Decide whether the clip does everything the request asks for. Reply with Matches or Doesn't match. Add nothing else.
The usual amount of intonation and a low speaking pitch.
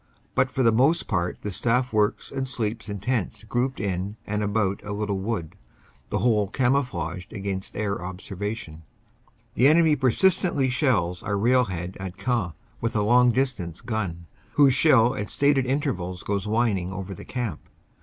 Matches